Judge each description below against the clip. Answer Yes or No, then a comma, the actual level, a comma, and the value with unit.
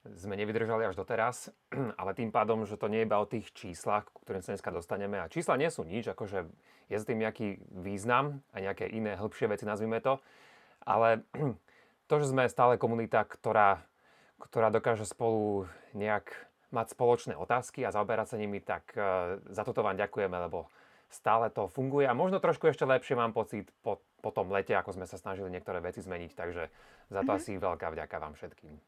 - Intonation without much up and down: No, average, 3.1 semitones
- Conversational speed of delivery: No, fast, 185 wpm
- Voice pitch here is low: Yes, low, 110 Hz